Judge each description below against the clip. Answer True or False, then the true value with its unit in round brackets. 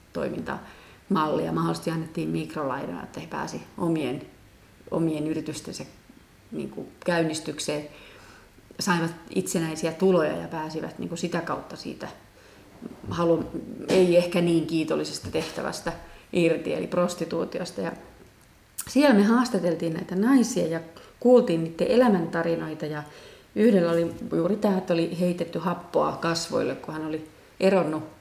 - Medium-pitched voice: True (165 Hz)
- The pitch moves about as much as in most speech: False (2.2 semitones)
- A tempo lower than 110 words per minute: False (115 wpm)